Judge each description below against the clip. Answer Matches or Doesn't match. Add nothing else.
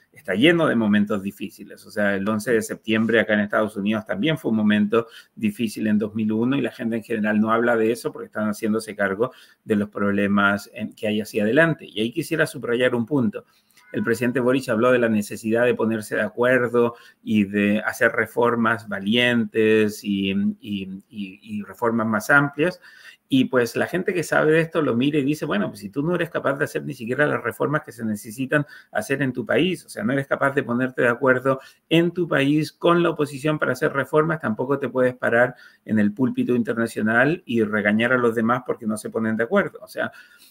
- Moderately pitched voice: Doesn't match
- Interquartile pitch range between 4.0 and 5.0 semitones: Matches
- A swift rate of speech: Matches